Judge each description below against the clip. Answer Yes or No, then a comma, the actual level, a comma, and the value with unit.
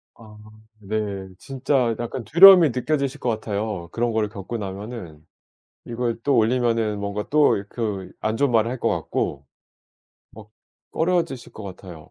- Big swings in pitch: No, average, 3.7 semitones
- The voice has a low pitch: Yes, low, 110 Hz